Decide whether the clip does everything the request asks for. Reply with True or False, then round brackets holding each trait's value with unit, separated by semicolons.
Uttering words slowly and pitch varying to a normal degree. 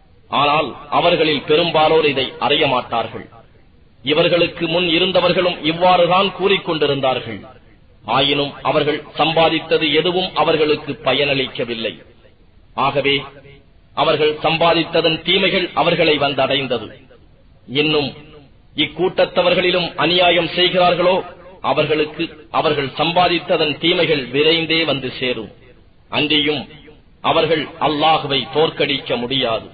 True (80 wpm; 3.9 semitones)